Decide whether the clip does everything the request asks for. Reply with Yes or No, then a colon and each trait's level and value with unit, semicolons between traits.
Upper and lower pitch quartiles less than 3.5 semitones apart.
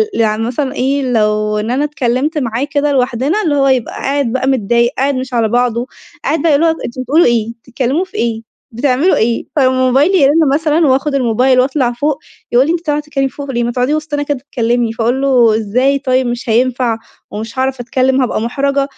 Yes: average, 3.1 semitones